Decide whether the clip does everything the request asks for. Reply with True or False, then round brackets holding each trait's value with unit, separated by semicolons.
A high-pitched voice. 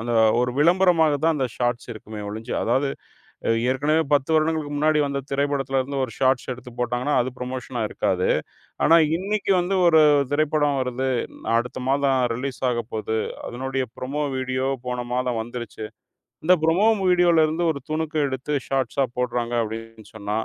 False (135 Hz)